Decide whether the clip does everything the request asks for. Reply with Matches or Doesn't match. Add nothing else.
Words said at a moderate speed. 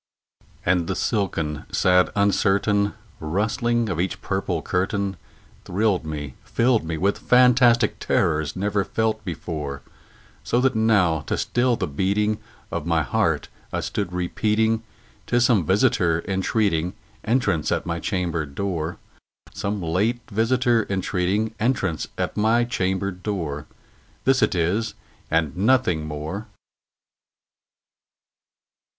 Doesn't match